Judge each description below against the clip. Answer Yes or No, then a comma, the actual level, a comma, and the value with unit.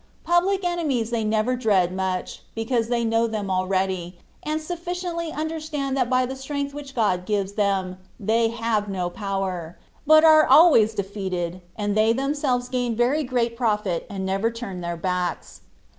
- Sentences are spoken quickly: No, average, 160 wpm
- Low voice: No, high, 225 Hz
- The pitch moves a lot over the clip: Yes, wide, 6.1 semitones